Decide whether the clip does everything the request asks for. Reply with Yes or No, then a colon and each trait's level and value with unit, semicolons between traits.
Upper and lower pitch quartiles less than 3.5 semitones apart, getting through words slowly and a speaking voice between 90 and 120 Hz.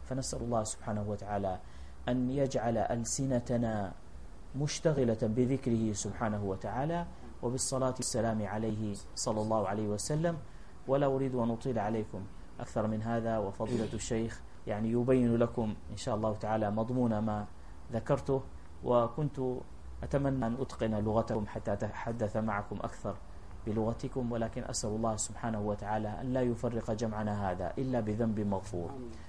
Yes: average, 2.9 semitones; slow, 125 wpm; low, 110 Hz